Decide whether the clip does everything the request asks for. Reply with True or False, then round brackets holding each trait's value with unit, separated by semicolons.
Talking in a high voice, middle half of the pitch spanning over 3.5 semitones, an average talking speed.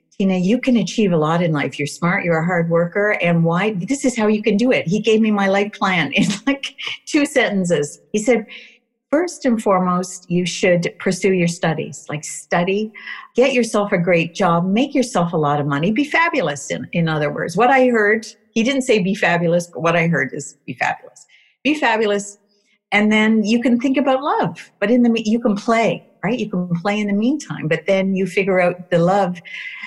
False (205 Hz; 5.0 semitones; 215 wpm)